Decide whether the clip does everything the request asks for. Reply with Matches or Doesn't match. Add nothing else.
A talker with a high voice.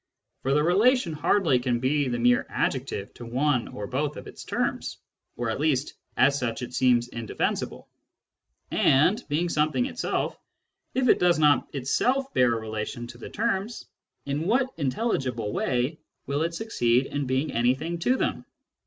Doesn't match